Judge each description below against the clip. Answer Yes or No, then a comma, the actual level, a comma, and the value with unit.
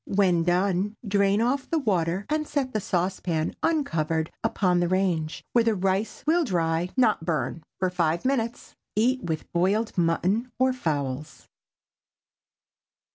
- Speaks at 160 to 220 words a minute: No, slow, 135 wpm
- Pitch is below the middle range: No, high, 190 Hz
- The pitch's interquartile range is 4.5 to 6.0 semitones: Yes, average, 5.3 semitones